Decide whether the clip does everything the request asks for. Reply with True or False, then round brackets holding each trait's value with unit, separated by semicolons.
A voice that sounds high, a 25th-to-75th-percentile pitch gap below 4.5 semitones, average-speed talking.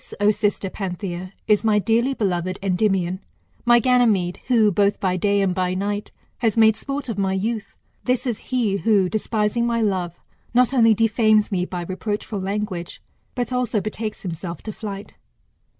True (210 Hz; 3.2 semitones; 160 wpm)